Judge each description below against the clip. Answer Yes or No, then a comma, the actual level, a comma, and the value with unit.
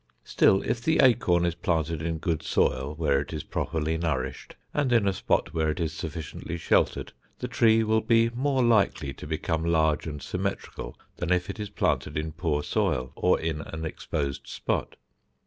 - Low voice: Yes, very low, 80 Hz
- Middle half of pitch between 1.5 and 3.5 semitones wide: No, average, 5.0 semitones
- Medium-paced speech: Yes, average, 180 wpm